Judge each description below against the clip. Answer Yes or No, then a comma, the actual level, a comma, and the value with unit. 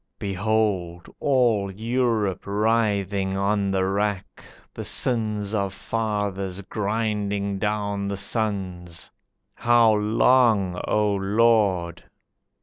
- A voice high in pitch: No, low, 100 Hz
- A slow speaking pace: Yes, slow, 90 wpm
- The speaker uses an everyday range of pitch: No, narrow, 2.1 semitones